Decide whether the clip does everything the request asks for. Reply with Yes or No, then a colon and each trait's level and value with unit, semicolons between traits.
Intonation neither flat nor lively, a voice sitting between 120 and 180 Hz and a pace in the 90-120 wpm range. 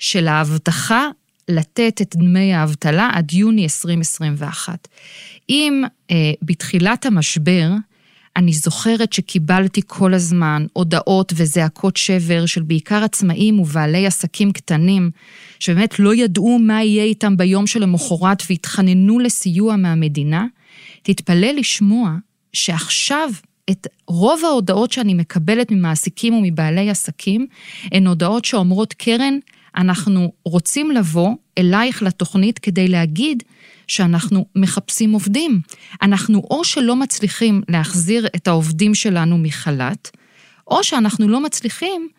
No: average, 4.0 semitones; high, 190 Hz; average, 110 wpm